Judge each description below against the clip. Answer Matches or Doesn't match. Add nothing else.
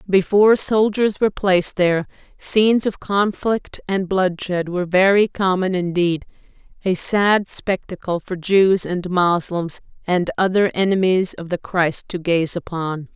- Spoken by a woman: Matches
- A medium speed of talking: Doesn't match